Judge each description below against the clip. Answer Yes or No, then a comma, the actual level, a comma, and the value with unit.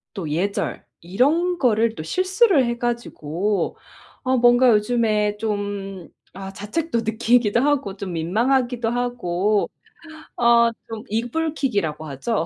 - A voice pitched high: Yes, high, 225 Hz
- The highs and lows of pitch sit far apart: No, average, 3.7 semitones